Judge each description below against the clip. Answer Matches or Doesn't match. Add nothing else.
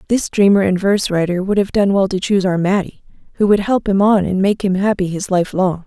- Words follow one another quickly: Matches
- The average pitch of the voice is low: Doesn't match